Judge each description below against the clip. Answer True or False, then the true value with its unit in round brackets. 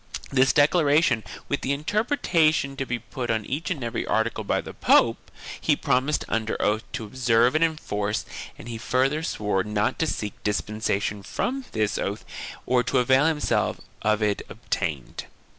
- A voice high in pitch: False (125 Hz)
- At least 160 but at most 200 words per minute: True (165 wpm)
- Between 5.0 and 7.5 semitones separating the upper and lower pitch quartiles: True (5.5 semitones)